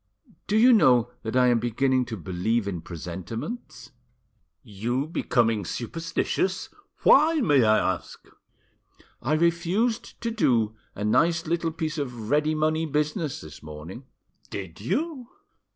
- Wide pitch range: Yes, wide, 7.2 semitones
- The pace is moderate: No, slow, 130 wpm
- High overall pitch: No, low, 130 Hz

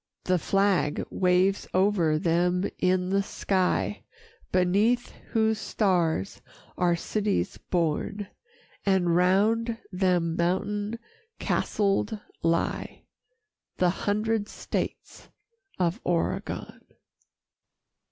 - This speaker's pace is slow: Yes, slow, 85 wpm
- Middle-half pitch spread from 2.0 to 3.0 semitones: Yes, narrow, 2.6 semitones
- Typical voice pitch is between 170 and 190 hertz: Yes, medium, 185 Hz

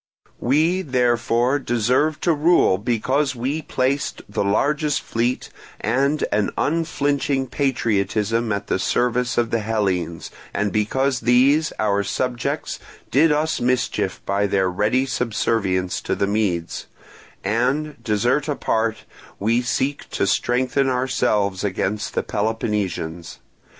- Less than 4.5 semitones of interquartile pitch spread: No, average, 4.8 semitones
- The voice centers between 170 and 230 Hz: No, low, 120 Hz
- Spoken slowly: Yes, slow, 120 wpm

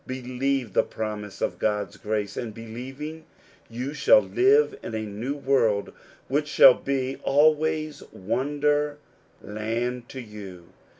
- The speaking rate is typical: No, slow, 125 wpm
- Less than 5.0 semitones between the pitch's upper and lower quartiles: No, average, 5.3 semitones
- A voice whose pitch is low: Yes, low, 125 Hz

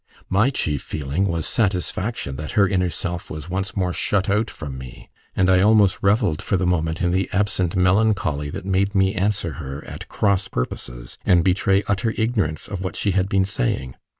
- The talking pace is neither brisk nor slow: Yes, average, 190 wpm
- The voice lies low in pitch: Yes, very low, 95 Hz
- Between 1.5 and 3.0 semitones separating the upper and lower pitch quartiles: No, average, 3.6 semitones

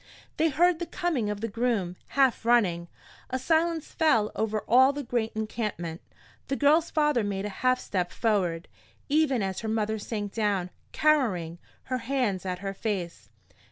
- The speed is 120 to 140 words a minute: No, average, 160 wpm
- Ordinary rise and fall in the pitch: No, wide, 5.8 semitones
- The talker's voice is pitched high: Yes, high, 225 Hz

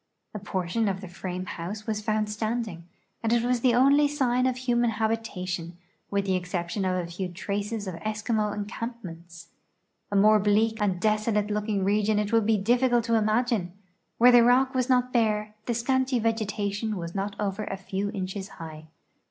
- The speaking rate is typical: Yes, average, 175 wpm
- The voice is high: Yes, high, 210 Hz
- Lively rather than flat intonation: No, average, 3.3 semitones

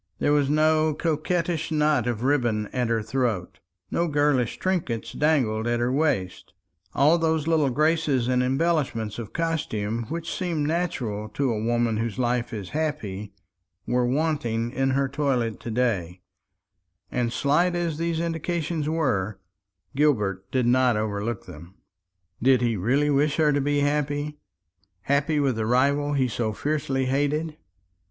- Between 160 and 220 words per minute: No, average, 145 wpm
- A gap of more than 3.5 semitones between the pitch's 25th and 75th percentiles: Yes, average, 4.8 semitones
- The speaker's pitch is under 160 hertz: Yes, low, 135 Hz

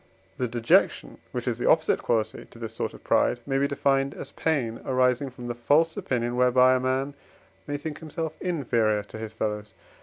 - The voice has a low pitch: Yes, low, 125 Hz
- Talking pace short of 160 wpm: No, average, 190 wpm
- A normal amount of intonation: Yes, average, 3.3 semitones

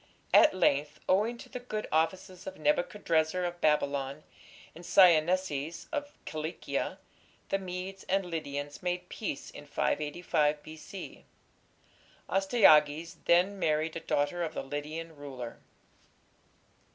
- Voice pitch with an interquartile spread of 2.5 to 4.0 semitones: Yes, average, 3.7 semitones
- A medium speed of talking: No, slow, 115 wpm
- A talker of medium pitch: Yes, medium, 165 Hz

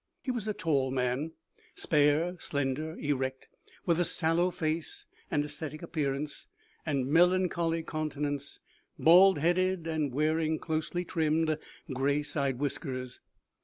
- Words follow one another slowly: Yes, slow, 120 wpm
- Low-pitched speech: No, medium, 155 Hz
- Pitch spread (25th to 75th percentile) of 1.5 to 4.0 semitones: Yes, average, 2.7 semitones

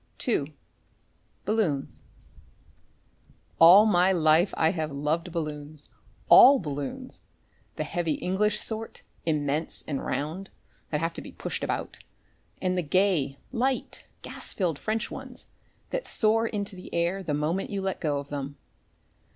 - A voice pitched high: No, medium, 170 Hz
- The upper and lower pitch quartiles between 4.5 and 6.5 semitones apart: Yes, average, 5.2 semitones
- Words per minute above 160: No, slow, 135 wpm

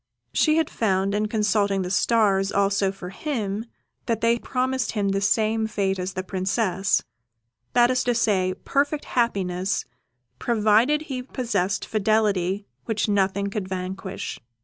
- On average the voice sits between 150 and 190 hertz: No, high, 205 Hz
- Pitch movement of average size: Yes, average, 3.2 semitones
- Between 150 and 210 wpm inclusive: No, average, 140 wpm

